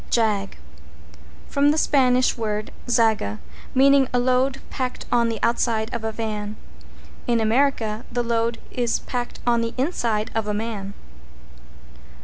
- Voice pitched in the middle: No, high, 230 Hz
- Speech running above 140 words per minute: No, slow, 135 wpm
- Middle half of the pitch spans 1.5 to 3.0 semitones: Yes, narrow, 2.4 semitones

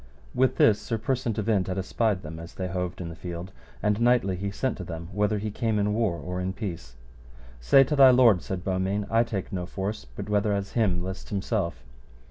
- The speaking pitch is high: No, low, 100 Hz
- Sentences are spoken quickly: Yes, fast, 220 wpm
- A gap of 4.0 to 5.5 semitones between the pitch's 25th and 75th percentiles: No, average, 3.5 semitones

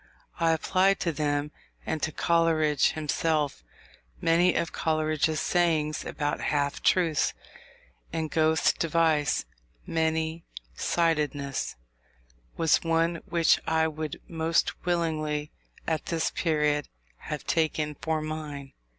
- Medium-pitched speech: Yes, medium, 160 Hz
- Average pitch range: No, narrow, 1.6 semitones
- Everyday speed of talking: No, slow, 105 wpm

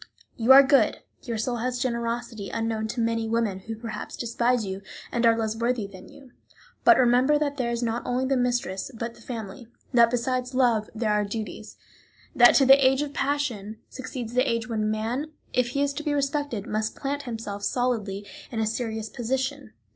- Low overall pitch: No, high, 235 Hz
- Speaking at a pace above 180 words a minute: Yes, average, 190 wpm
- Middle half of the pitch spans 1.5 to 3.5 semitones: Yes, average, 2.8 semitones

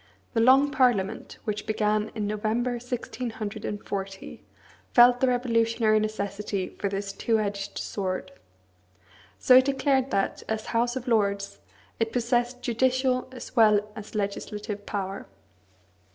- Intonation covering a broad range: No, average, 3.2 semitones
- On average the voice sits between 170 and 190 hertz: No, high, 220 Hz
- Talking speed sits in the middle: No, slow, 125 wpm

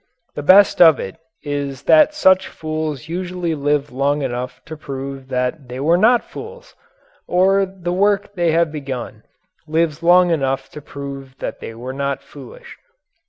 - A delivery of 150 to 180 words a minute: Yes, average, 155 wpm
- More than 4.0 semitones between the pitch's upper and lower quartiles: Yes, average, 4.7 semitones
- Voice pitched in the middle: Yes, medium, 155 Hz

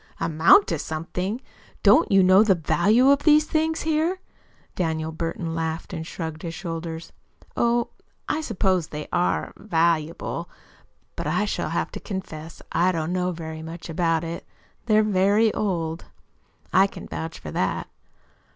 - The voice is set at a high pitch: No, medium, 175 Hz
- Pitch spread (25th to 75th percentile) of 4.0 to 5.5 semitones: Yes, average, 4.3 semitones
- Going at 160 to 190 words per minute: No, average, 150 wpm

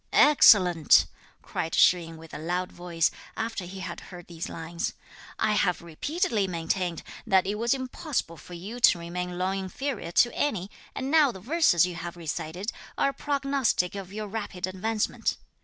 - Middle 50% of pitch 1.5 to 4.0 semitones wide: No, average, 4.6 semitones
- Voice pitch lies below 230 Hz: Yes, medium, 185 Hz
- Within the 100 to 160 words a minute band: No, average, 170 wpm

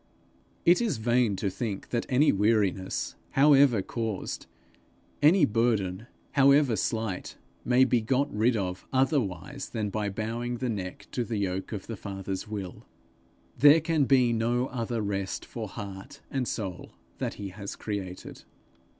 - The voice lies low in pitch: Yes, low, 115 Hz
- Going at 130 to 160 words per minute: Yes, average, 145 wpm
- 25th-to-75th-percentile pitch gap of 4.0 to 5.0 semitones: Yes, average, 4.3 semitones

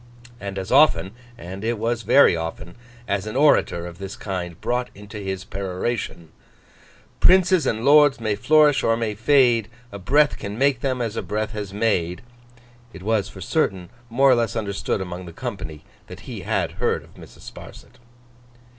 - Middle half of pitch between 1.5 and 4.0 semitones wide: No, average, 4.5 semitones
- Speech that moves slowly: No, average, 170 wpm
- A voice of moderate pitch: No, low, 105 Hz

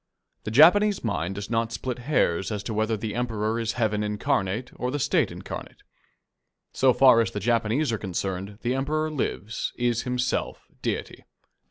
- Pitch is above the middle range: No, low, 115 Hz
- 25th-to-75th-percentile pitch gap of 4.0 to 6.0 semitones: No, average, 3.3 semitones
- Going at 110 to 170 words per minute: Yes, average, 165 wpm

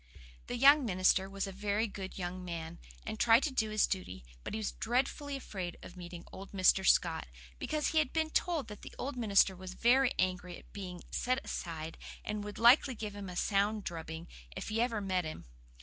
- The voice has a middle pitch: No, high, 200 Hz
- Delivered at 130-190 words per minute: No, fast, 205 wpm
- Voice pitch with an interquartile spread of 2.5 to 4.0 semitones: No, average, 4.7 semitones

